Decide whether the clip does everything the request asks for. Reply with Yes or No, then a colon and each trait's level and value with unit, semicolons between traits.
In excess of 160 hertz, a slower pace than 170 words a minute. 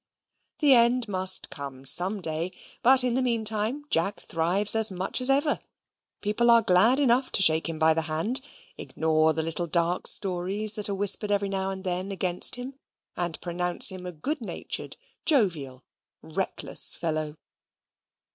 Yes: high, 190 Hz; average, 160 wpm